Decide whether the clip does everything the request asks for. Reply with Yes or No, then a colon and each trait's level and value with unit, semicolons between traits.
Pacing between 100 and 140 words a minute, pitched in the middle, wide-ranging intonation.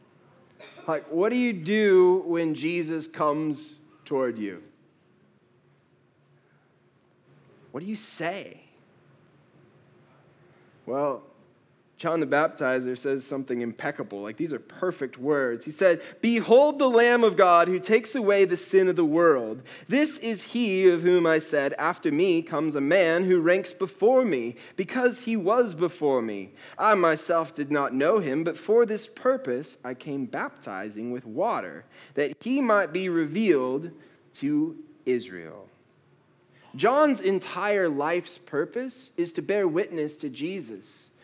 Yes: slow, 135 wpm; medium, 175 Hz; wide, 7.4 semitones